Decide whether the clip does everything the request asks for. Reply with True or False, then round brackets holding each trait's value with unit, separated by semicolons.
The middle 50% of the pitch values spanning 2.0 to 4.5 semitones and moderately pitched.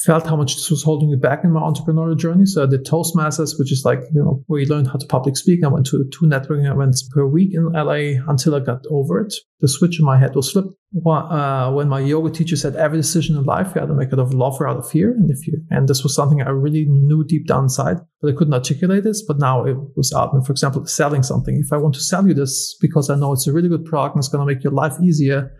True (2.5 semitones; 150 Hz)